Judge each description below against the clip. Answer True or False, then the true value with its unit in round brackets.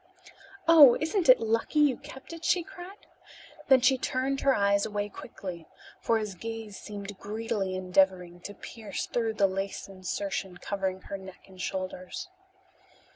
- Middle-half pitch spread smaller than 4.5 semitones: False (5.2 semitones)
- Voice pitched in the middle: False (205 Hz)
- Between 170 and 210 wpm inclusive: False (150 wpm)